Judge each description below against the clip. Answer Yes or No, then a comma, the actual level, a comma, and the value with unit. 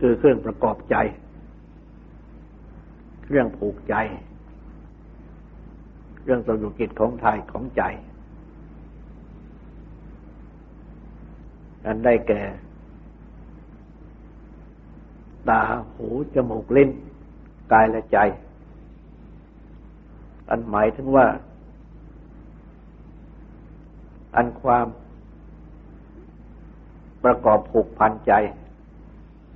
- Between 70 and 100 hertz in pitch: No, low, 110 Hz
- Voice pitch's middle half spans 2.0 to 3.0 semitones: Yes, average, 2.7 semitones